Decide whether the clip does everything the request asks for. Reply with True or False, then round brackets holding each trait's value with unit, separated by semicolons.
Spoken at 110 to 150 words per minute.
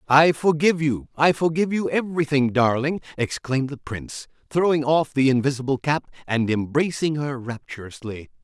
True (140 wpm)